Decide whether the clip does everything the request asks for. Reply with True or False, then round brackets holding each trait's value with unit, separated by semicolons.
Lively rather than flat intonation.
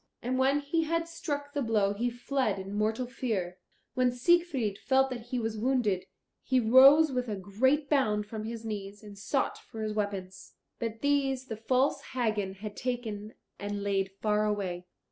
False (4.3 semitones)